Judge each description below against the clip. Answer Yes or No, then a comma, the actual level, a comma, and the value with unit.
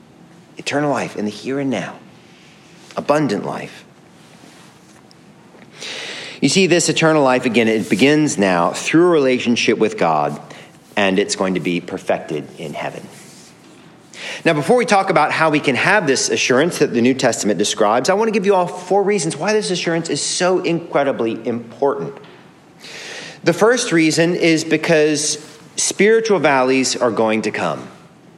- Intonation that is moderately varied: No, wide, 5.9 semitones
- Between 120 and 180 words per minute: Yes, average, 155 wpm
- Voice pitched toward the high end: No, medium, 150 Hz